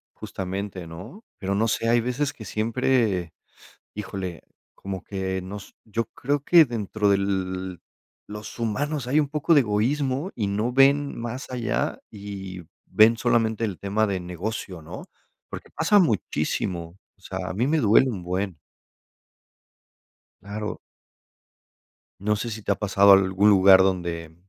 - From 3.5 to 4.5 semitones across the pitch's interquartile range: Yes, average, 3.9 semitones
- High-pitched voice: No, low, 105 Hz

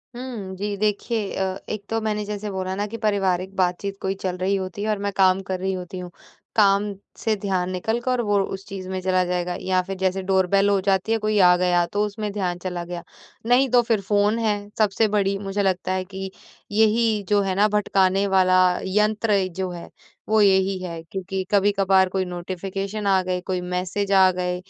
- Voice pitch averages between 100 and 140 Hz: No, high, 195 Hz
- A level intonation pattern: Yes, narrow, 1.9 semitones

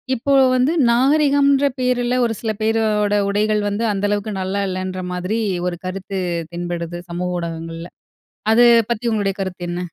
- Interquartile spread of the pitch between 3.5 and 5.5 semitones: Yes, average, 4.2 semitones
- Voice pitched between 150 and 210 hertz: Yes, high, 205 Hz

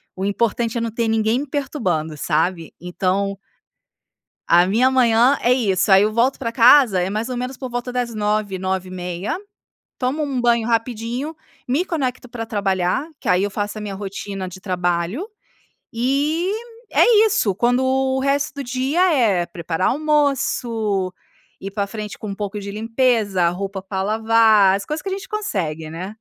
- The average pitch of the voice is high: Yes, high, 220 Hz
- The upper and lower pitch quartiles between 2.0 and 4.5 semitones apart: No, average, 4.9 semitones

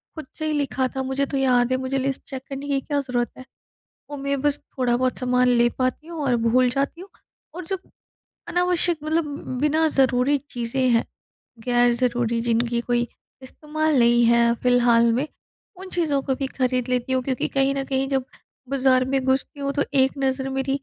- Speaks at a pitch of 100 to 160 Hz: No, very high, 265 Hz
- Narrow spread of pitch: Yes, narrow, 2.3 semitones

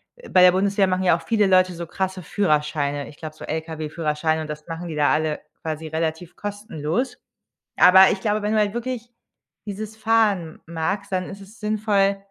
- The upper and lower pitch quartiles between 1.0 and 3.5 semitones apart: No, average, 4.5 semitones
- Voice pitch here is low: No, medium, 185 Hz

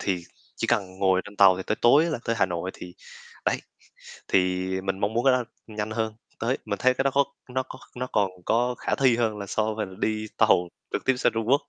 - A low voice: Yes, low, 110 Hz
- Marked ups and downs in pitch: No, average, 4.3 semitones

